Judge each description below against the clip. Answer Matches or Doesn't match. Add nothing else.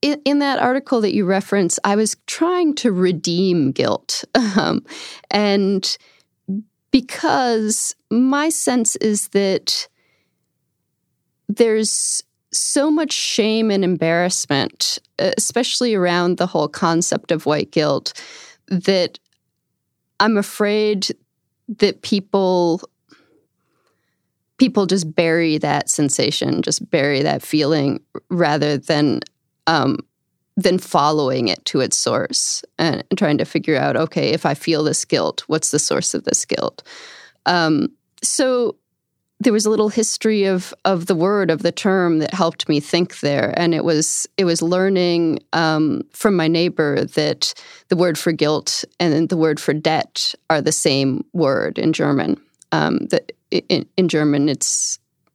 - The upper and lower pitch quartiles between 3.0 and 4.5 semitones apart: Doesn't match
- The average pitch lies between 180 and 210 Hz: Matches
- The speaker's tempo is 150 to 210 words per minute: Doesn't match